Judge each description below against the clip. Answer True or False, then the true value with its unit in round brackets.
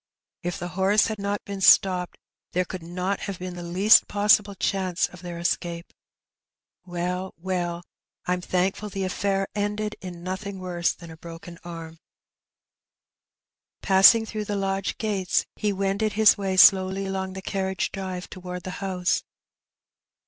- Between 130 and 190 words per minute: True (150 wpm)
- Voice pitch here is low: False (190 Hz)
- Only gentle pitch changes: True (1.9 semitones)